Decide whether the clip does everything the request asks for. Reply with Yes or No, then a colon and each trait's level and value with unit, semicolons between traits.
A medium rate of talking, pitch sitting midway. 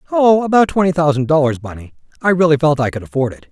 Yes: average, 190 wpm; medium, 150 Hz